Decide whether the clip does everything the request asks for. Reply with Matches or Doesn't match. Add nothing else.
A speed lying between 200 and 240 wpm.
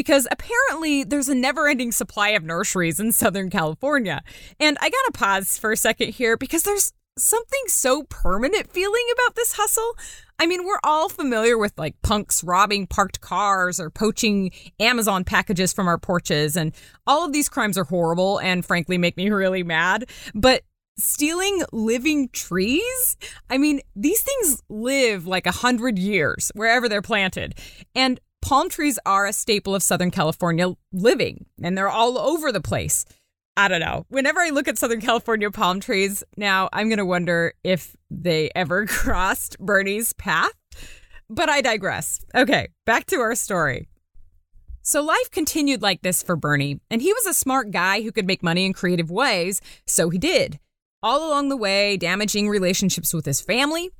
Doesn't match